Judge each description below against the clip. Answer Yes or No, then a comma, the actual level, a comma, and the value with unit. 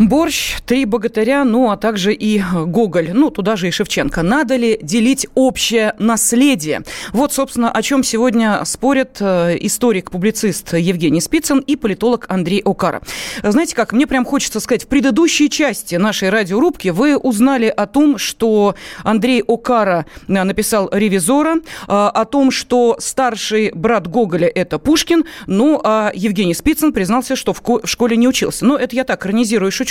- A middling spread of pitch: Yes, average, 4.4 semitones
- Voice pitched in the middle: No, high, 230 Hz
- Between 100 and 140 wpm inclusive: No, average, 150 wpm